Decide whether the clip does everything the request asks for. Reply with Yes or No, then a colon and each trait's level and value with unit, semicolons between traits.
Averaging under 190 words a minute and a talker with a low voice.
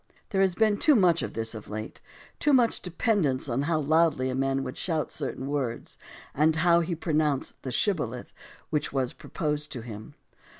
No: average, 180 wpm; medium, 150 Hz